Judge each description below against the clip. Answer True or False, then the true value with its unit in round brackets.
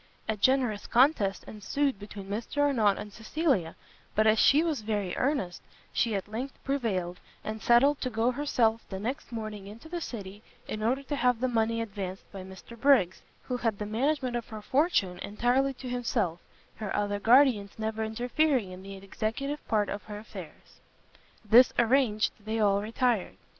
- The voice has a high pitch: True (225 Hz)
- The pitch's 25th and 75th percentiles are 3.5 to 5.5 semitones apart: True (4.0 semitones)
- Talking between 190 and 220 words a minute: False (170 wpm)